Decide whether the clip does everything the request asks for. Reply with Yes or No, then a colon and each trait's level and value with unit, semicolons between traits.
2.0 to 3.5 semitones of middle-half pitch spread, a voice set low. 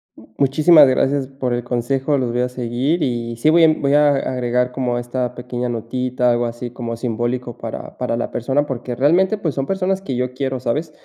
Yes: average, 2.7 semitones; low, 125 Hz